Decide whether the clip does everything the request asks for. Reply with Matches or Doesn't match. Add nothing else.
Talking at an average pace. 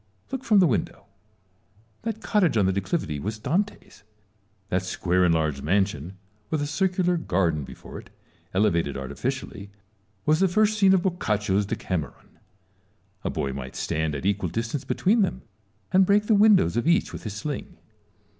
Matches